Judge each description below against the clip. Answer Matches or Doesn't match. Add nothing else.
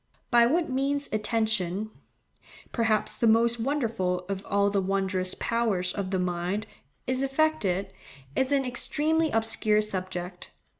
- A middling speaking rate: Doesn't match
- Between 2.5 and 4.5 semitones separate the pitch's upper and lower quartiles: Doesn't match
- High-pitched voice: Matches